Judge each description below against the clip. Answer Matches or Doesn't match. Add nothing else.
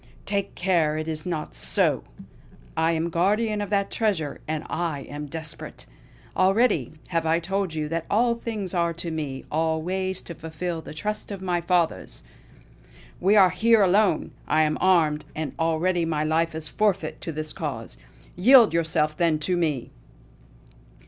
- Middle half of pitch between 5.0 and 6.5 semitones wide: Doesn't match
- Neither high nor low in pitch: Matches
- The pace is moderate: Matches